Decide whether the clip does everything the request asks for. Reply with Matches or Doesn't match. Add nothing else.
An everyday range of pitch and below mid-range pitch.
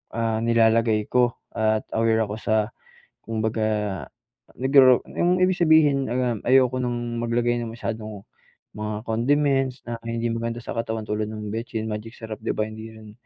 Doesn't match